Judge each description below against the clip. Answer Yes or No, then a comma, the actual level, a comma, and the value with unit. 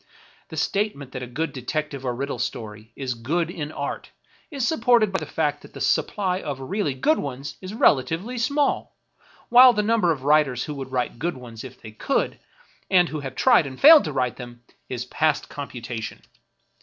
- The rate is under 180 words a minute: No, average, 190 wpm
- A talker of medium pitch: Yes, medium, 145 Hz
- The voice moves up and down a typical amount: No, wide, 7.3 semitones